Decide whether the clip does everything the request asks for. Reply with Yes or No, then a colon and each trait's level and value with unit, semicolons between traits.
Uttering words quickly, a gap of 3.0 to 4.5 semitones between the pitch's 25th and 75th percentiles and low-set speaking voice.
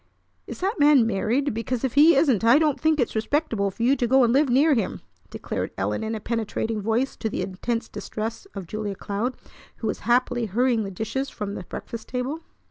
No: fast, 210 wpm; average, 3.6 semitones; high, 235 Hz